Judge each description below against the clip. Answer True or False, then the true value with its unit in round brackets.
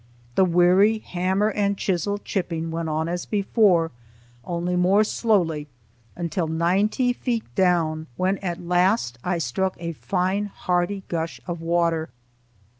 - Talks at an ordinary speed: False (130 wpm)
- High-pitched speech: False (180 Hz)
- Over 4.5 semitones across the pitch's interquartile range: False (2.9 semitones)